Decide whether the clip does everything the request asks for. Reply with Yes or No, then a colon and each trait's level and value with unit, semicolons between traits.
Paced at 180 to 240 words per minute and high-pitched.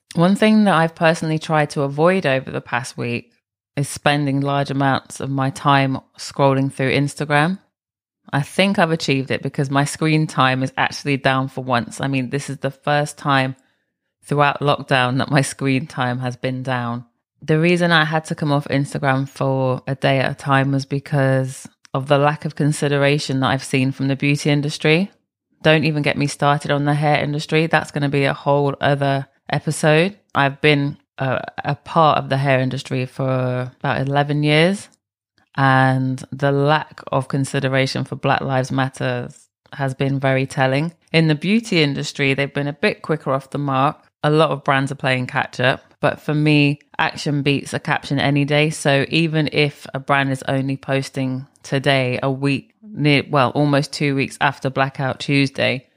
No: average, 185 wpm; medium, 140 Hz